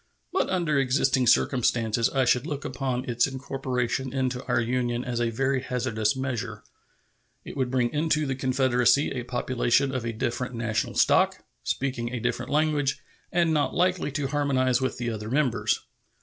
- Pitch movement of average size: No, narrow, 2.3 semitones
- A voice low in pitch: Yes, low, 130 Hz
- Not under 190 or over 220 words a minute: No, average, 165 wpm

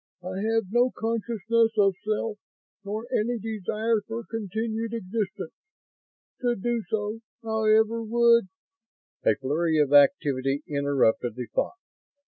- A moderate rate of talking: No, slow, 120 wpm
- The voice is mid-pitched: No, high, 215 Hz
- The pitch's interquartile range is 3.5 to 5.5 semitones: Yes, average, 3.8 semitones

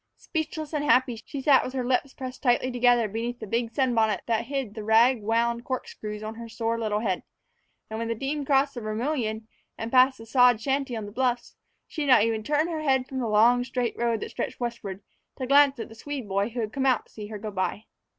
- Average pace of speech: No, fast, 235 wpm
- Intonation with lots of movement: No, average, 3.1 semitones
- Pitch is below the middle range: No, high, 240 Hz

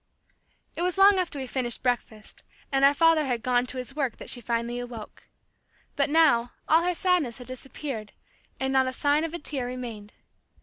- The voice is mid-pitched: No, very high, 260 Hz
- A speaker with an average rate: Yes, average, 190 wpm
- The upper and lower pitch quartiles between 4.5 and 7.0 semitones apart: No, average, 4.1 semitones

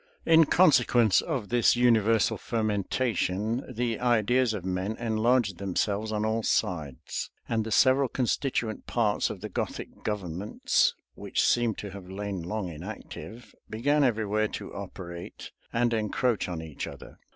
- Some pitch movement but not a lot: Yes, average, 3.4 semitones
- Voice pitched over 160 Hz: No, low, 110 Hz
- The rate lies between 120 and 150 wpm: Yes, average, 140 wpm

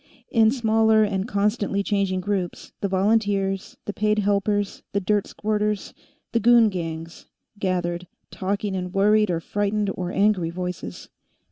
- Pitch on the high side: Yes, high, 200 Hz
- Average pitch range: No, narrow, 2.3 semitones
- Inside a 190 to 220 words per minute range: No, slow, 135 wpm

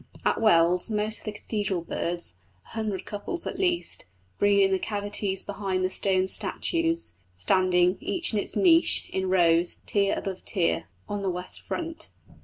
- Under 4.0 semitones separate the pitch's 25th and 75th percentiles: Yes, average, 2.8 semitones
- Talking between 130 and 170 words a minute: Yes, average, 165 wpm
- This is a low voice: No, high, 195 Hz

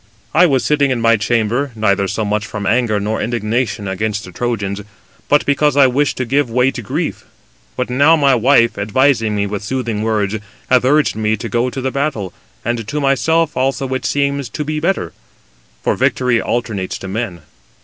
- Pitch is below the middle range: Yes, low, 120 Hz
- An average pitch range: Yes, average, 4.5 semitones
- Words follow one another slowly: No, average, 180 wpm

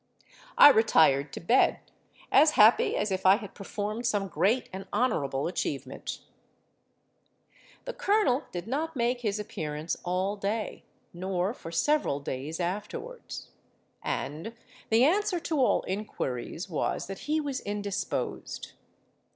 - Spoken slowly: Yes, slow, 125 wpm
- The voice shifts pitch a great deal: Yes, wide, 6.4 semitones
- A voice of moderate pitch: No, high, 205 Hz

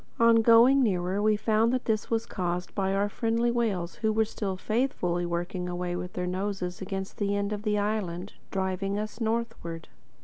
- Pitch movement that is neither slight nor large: Yes, average, 3.7 semitones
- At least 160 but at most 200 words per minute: Yes, average, 180 wpm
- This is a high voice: Yes, high, 205 Hz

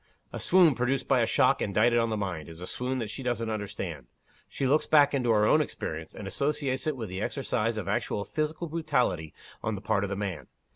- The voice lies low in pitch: Yes, low, 115 Hz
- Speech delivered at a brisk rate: Yes, fast, 225 wpm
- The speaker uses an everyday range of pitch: No, wide, 5.7 semitones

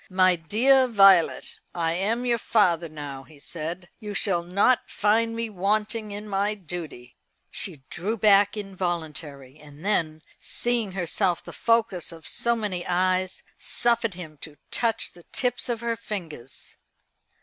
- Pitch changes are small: No, average, 4.6 semitones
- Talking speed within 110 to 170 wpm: Yes, average, 145 wpm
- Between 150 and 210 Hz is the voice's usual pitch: Yes, high, 190 Hz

